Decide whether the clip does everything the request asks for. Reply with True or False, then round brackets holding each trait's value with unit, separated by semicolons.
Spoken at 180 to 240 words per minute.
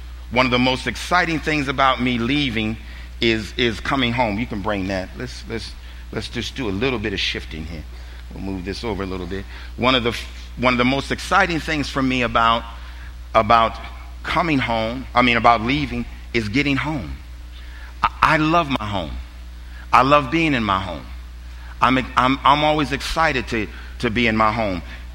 True (190 wpm)